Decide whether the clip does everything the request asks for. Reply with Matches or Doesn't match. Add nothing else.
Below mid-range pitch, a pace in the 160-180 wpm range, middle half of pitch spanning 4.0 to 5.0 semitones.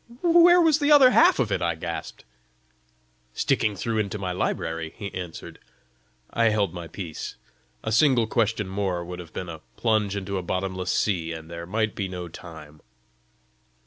Matches